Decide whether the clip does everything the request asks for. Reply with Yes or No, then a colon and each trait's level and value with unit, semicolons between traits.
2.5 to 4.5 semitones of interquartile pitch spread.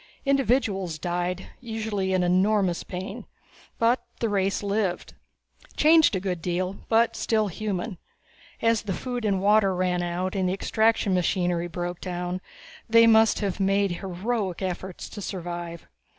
Yes: average, 3.4 semitones